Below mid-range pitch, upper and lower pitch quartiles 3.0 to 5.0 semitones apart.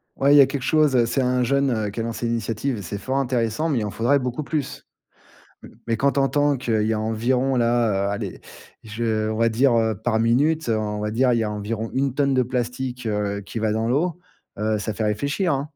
Yes: low, 120 Hz; average, 3.7 semitones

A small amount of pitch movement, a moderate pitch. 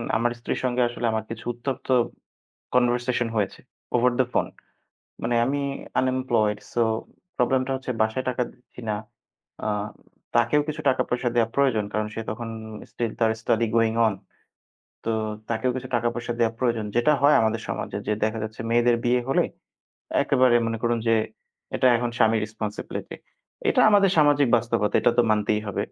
No: narrow, 2.3 semitones; low, 120 Hz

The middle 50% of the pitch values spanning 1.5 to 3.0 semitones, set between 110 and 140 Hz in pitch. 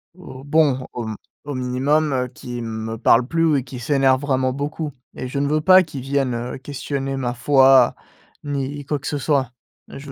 Yes: narrow, 2.4 semitones; low, 135 Hz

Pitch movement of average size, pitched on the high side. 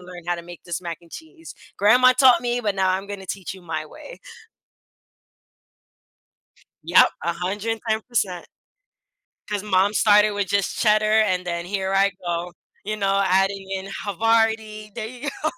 Yes: average, 3.0 semitones; high, 200 Hz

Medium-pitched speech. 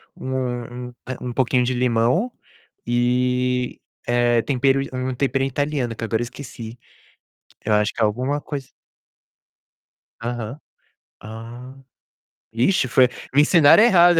No: low, 125 Hz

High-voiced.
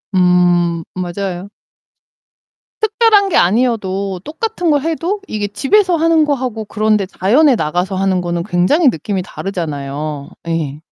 Yes: high, 200 Hz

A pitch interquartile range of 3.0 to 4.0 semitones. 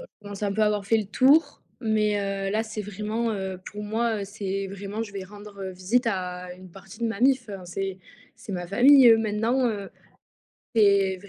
No: narrow, 2.4 semitones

